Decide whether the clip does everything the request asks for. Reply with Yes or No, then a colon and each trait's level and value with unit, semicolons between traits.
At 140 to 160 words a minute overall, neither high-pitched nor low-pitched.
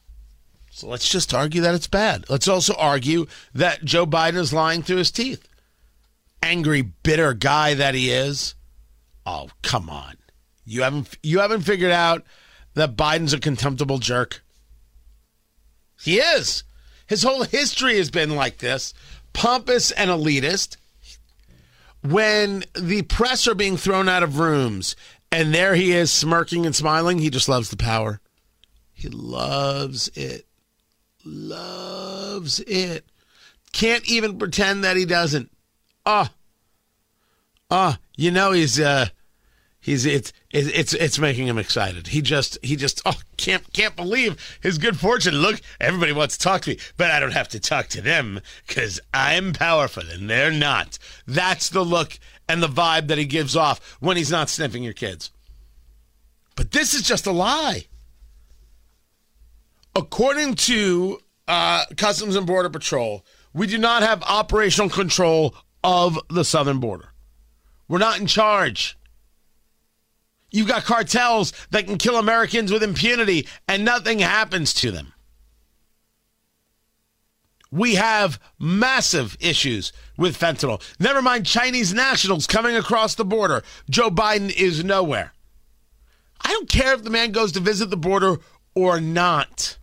Yes: average, 145 wpm; medium, 160 Hz